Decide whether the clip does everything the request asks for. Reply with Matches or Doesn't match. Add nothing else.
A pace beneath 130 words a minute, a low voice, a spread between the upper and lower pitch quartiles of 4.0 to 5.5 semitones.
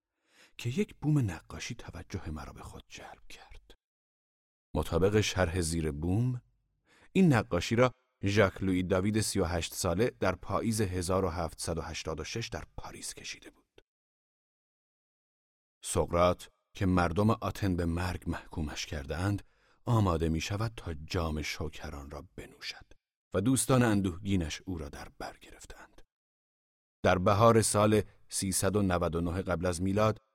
Matches